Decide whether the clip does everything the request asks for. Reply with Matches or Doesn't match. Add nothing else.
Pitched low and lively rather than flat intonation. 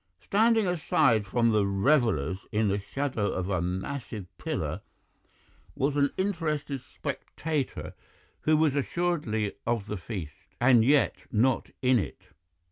Matches